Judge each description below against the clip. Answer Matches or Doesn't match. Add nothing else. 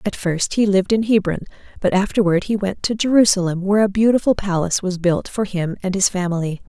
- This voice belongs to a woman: Matches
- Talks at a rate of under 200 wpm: Doesn't match